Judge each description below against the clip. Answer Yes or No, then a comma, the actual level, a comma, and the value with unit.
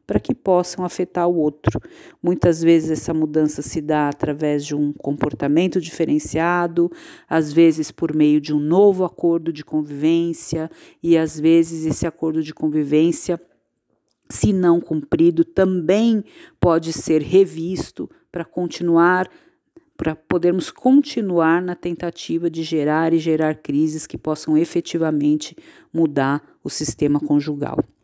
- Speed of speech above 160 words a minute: No, average, 130 wpm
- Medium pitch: Yes, medium, 165 Hz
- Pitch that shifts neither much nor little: No, narrow, 2.3 semitones